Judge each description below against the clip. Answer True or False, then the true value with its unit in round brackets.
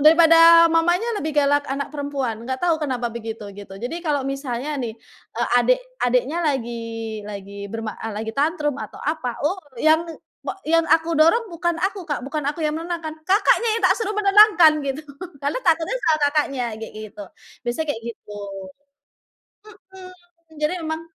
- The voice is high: True (300 Hz)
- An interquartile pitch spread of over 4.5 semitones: True (5.1 semitones)